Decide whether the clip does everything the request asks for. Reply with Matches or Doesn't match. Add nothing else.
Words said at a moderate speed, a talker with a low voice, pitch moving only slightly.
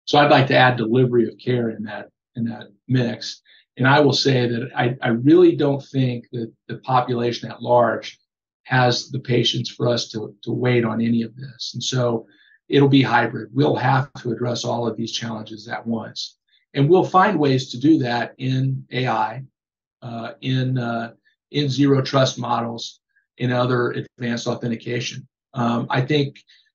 Matches